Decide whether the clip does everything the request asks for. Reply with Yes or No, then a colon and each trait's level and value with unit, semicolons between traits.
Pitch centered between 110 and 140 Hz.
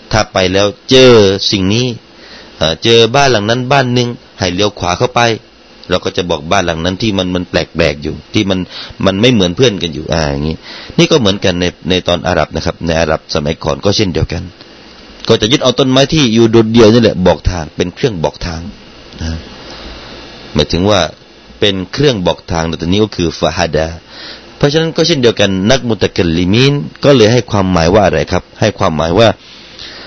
No: low, 100 Hz